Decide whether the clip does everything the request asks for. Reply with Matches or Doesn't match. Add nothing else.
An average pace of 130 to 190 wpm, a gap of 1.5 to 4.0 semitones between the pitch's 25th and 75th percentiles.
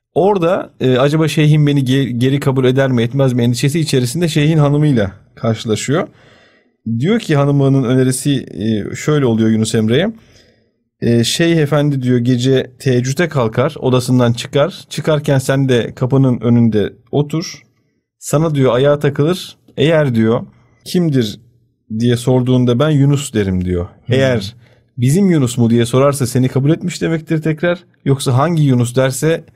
Matches